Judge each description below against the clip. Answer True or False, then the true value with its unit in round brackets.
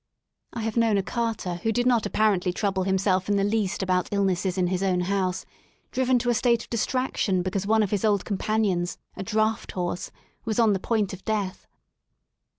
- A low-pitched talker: False (200 Hz)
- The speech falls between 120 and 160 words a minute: False (200 wpm)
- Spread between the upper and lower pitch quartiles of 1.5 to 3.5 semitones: True (3.0 semitones)